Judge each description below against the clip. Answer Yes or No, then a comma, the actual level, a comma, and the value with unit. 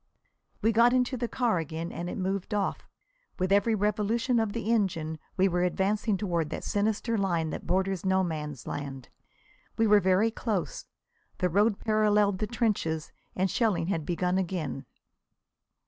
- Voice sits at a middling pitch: No, high, 195 Hz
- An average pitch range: Yes, average, 3.9 semitones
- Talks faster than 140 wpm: Yes, average, 160 wpm